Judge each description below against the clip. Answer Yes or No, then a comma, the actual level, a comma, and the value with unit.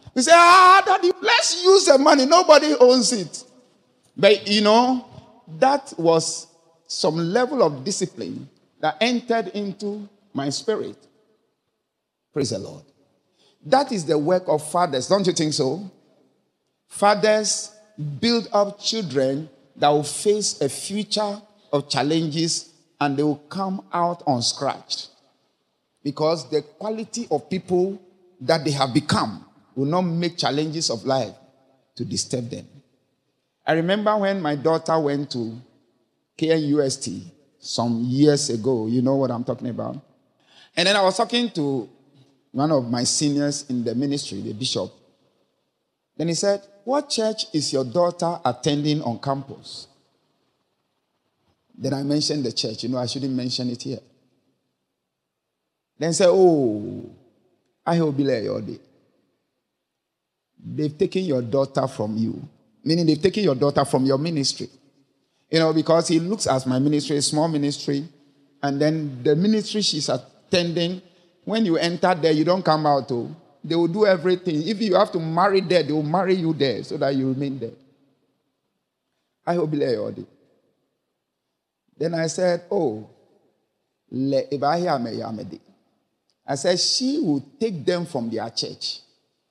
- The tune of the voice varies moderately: No, wide, 5.8 semitones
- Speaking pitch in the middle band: Yes, medium, 160 Hz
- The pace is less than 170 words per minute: Yes, average, 150 wpm